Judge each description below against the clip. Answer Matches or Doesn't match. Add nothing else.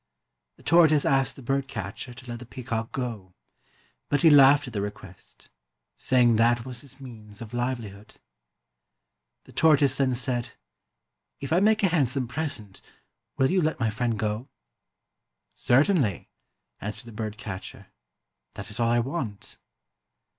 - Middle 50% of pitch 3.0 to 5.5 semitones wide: Matches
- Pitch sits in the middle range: Doesn't match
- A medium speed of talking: Matches